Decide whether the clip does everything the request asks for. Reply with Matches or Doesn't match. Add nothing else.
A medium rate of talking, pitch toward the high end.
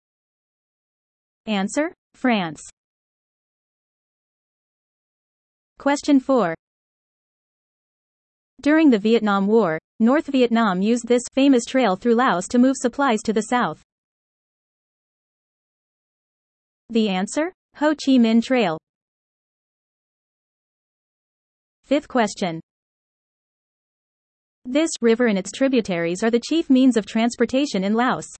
Doesn't match